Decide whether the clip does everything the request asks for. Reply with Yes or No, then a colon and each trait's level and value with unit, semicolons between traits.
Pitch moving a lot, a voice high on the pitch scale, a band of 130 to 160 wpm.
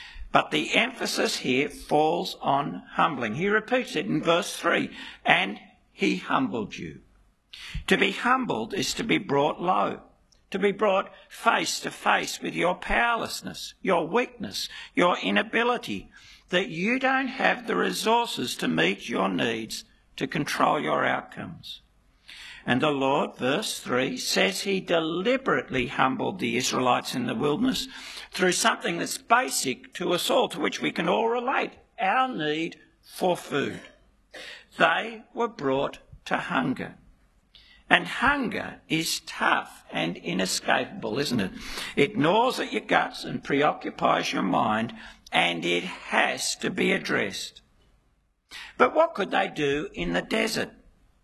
Yes: wide, 7.7 semitones; high, 200 Hz; average, 140 wpm